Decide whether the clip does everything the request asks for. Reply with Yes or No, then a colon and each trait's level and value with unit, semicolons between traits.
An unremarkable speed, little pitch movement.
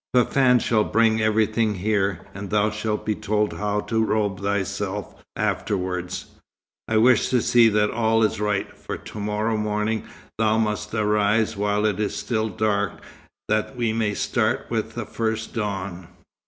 Yes: average, 155 wpm; narrow, 1.3 semitones